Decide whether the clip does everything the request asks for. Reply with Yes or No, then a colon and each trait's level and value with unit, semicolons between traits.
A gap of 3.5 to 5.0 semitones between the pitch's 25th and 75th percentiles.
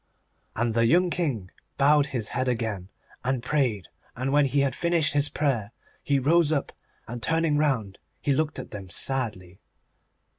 Yes: average, 4.5 semitones